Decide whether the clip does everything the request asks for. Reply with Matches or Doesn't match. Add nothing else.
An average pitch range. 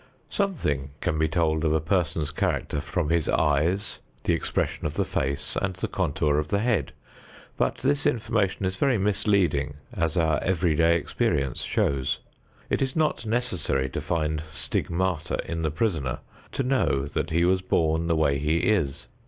Matches